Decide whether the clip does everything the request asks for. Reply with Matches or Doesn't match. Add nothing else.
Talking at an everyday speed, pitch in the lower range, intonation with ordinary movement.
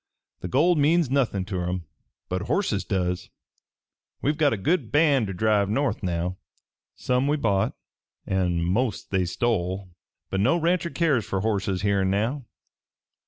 Doesn't match